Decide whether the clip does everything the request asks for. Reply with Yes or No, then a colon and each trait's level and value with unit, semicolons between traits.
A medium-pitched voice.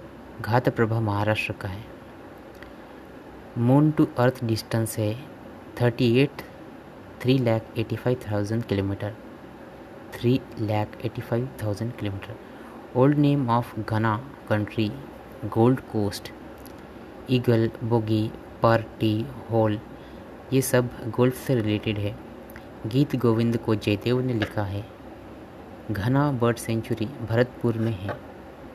No: low, 115 Hz